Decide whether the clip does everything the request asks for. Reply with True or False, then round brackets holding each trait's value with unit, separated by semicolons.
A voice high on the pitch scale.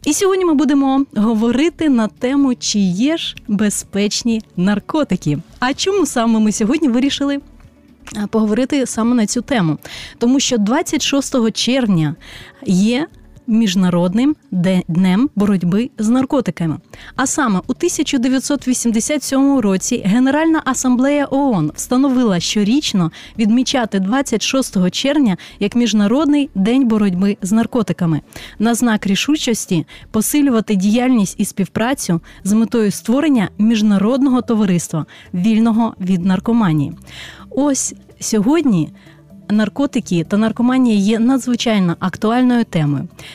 True (230 Hz)